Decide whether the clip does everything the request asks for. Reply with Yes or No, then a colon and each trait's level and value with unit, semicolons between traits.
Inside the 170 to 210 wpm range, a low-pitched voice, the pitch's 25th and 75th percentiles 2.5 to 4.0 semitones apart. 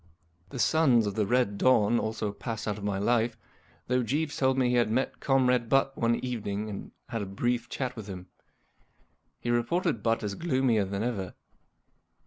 Yes: average, 180 wpm; low, 115 Hz; average, 3.5 semitones